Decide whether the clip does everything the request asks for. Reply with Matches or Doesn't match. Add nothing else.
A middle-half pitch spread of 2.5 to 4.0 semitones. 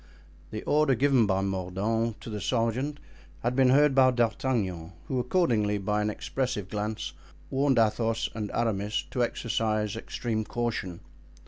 Matches